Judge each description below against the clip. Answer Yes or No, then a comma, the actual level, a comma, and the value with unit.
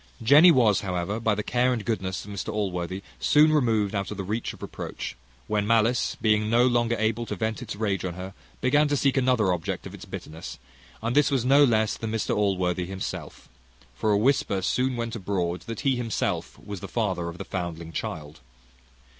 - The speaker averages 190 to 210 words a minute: Yes, average, 200 wpm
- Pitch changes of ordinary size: Yes, average, 4.2 semitones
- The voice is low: Yes, low, 110 Hz